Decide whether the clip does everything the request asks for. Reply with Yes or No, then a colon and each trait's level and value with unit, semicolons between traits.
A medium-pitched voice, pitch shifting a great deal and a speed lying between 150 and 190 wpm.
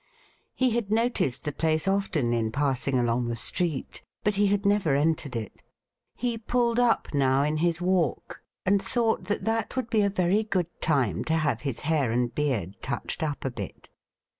Yes: medium, 160 Hz; wide, 7.5 semitones; average, 185 wpm